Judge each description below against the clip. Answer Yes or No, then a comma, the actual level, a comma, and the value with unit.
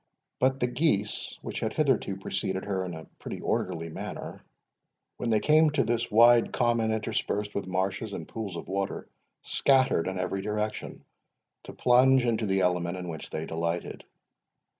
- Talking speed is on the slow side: No, average, 160 wpm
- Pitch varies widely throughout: No, average, 4.4 semitones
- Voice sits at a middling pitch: No, low, 105 Hz